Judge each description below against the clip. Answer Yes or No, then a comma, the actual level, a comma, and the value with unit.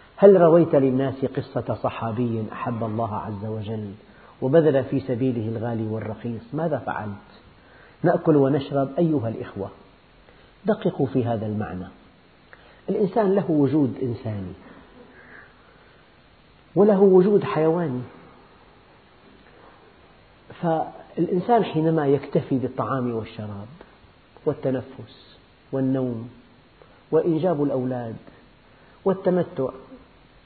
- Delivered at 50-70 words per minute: No, average, 80 wpm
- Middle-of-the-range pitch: No, low, 130 Hz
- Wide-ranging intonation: Yes, wide, 6.0 semitones